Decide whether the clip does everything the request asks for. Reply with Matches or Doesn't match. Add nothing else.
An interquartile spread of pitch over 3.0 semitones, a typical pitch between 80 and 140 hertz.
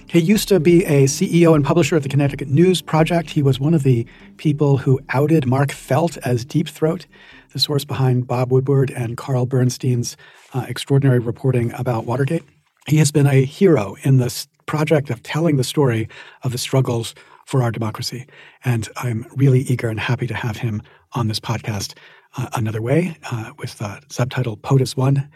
Matches